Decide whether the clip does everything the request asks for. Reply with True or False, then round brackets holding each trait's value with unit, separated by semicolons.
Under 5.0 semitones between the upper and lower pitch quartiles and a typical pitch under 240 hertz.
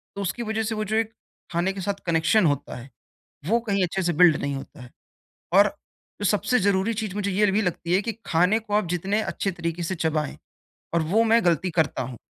True (4.0 semitones; 190 Hz)